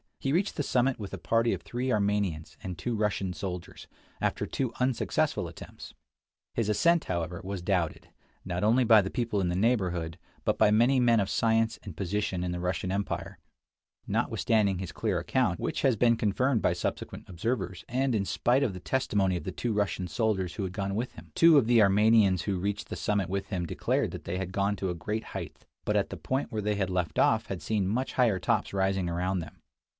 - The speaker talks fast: Yes, fast, 215 wpm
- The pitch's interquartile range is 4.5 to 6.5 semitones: No, average, 4.0 semitones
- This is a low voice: Yes, low, 100 Hz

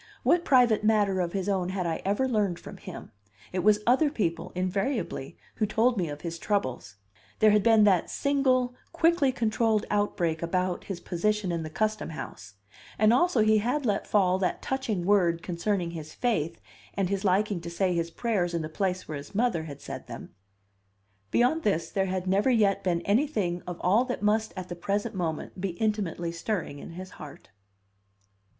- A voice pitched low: No, high, 195 Hz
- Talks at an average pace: Yes, average, 185 wpm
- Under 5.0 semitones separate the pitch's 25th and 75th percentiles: Yes, average, 4.1 semitones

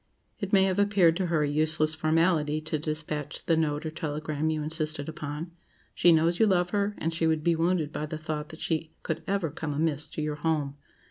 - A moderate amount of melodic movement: No, narrow, 1.8 semitones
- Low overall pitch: No, medium, 160 Hz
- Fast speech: Yes, fast, 215 wpm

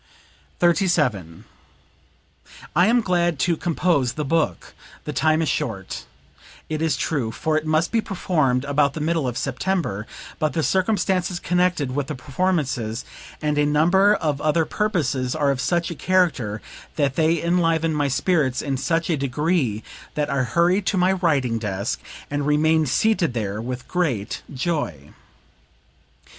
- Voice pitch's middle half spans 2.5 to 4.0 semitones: No, average, 5.0 semitones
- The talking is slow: No, average, 150 wpm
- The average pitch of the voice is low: No, medium, 155 Hz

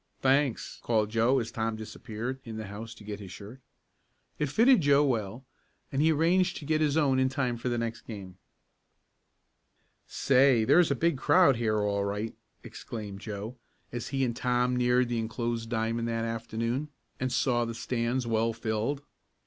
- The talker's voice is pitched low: Yes, low, 120 Hz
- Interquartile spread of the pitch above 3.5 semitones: No, average, 3.1 semitones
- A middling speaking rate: Yes, average, 175 wpm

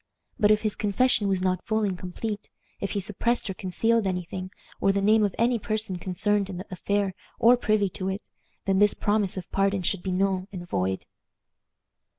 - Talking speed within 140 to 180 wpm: No, average, 195 wpm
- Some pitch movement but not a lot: No, narrow, 2.3 semitones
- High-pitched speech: Yes, high, 195 Hz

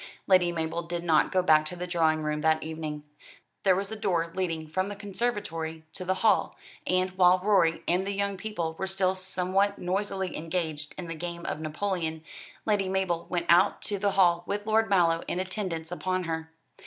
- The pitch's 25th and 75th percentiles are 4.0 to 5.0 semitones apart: No, average, 2.8 semitones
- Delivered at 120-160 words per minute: No, average, 190 wpm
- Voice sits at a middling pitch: Yes, medium, 180 Hz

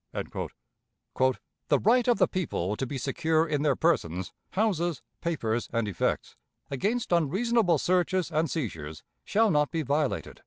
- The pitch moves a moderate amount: No, wide, 6.1 semitones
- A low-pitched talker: No, medium, 155 Hz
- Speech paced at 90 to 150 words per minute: Yes, average, 140 wpm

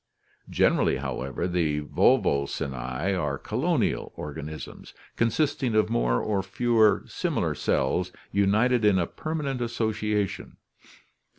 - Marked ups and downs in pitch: Yes, wide, 7.6 semitones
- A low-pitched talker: Yes, low, 100 Hz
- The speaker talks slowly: Yes, slow, 105 wpm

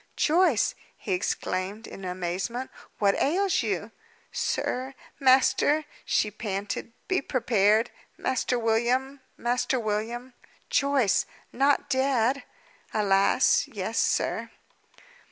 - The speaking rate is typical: No, slow, 100 wpm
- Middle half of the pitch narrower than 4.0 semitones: No, average, 4.4 semitones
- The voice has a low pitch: No, high, 240 Hz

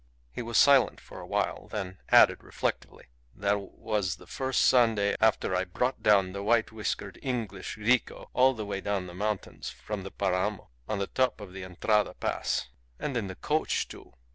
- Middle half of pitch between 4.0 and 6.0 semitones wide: No, average, 3.3 semitones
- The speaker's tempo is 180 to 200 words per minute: Yes, average, 185 wpm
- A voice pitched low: Yes, low, 105 Hz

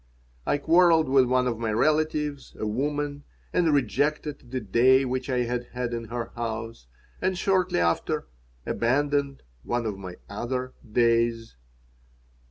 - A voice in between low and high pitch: No, low, 125 Hz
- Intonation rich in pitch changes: No, average, 3.8 semitones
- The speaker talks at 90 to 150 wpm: Yes, average, 140 wpm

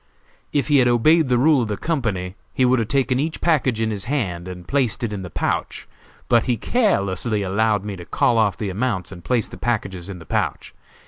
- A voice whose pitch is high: No, low, 110 Hz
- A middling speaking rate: No, fast, 220 wpm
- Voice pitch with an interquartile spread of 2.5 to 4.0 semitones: No, average, 5.1 semitones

